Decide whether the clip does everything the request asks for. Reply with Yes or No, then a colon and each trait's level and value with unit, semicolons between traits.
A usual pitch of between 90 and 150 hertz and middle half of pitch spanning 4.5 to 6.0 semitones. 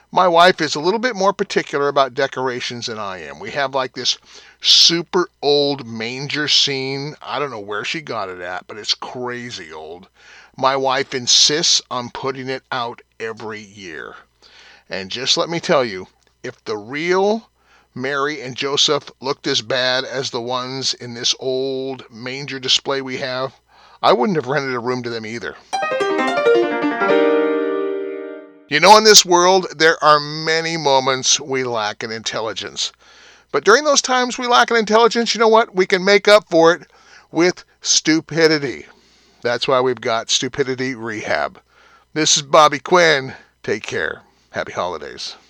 Yes: medium, 140 Hz; average, 4.9 semitones